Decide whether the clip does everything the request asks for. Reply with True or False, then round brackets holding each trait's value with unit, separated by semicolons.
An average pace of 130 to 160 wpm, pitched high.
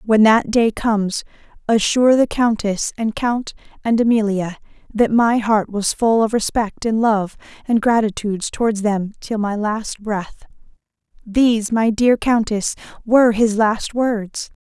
True (150 wpm; 220 Hz)